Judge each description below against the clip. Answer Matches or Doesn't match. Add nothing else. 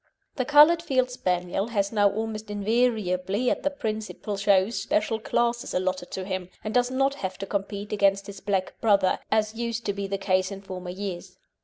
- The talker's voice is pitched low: Doesn't match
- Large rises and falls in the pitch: Doesn't match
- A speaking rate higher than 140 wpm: Matches